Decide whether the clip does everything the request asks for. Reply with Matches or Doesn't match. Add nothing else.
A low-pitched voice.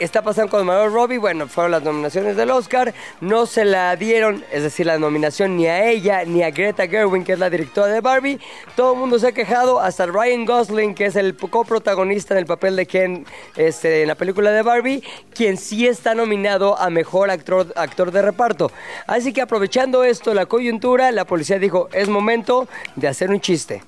Doesn't match